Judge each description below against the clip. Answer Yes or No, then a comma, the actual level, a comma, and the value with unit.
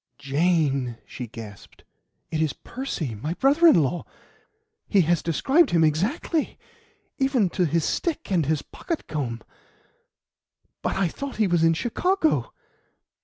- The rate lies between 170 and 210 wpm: No, slow, 135 wpm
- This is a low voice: No, medium, 170 Hz